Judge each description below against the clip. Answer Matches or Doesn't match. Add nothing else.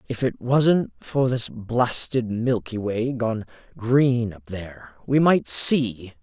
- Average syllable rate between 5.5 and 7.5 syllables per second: Doesn't match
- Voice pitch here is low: Matches